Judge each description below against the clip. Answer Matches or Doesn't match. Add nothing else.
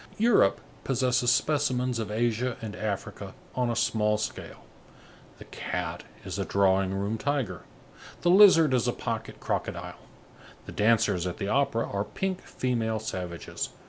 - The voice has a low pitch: Matches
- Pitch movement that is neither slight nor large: Matches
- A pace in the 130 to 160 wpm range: Matches